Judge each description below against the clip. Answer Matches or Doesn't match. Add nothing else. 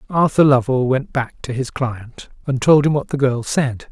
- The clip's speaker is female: Doesn't match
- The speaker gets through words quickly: Matches